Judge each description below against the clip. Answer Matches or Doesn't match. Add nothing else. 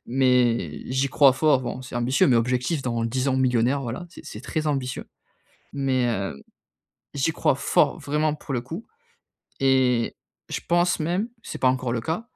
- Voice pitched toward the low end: Matches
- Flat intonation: Doesn't match